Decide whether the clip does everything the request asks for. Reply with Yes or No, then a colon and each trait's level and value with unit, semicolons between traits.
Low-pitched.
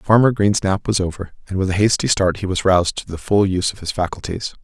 Yes: very low, 95 Hz